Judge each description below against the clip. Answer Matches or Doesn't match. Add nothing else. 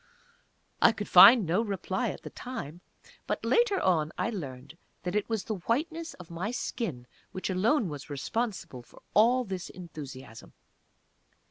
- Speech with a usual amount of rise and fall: Doesn't match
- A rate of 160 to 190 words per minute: Doesn't match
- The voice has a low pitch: Doesn't match